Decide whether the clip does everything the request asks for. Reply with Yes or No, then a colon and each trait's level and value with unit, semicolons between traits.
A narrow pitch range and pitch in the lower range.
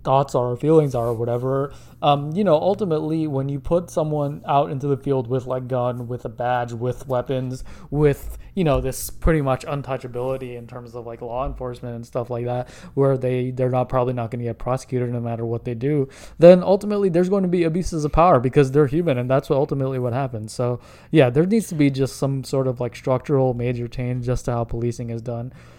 No: average, 3.0 semitones; low, 130 Hz